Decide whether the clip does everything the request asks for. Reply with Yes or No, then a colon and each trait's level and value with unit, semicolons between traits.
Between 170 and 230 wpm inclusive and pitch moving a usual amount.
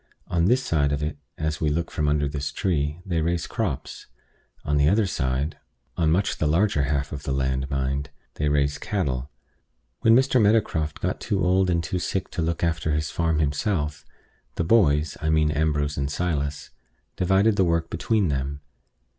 Yes: average, 180 wpm; average, 3.5 semitones